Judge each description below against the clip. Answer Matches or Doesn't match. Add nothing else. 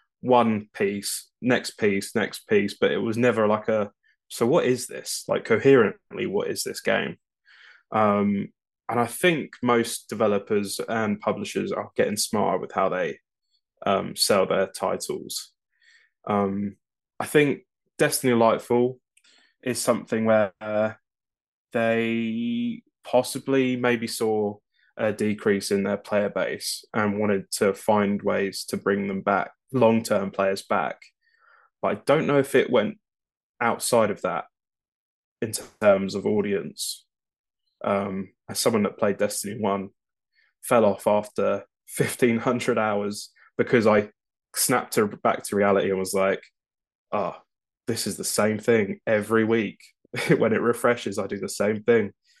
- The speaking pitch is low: Matches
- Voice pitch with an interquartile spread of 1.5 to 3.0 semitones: Doesn't match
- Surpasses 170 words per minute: Doesn't match